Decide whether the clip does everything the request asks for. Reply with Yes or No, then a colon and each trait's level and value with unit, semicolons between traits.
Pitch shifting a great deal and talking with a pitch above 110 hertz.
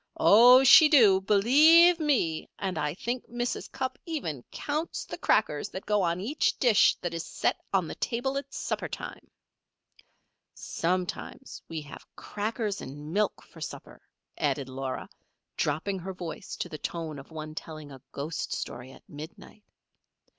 Yes: wide, 7.9 semitones; high, 190 Hz